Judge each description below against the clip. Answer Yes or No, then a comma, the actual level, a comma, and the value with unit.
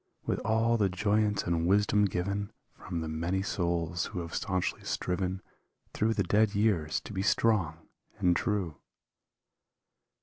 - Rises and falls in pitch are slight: No, average, 3.2 semitones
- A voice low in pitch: Yes, very low, 95 Hz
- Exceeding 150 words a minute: No, average, 140 wpm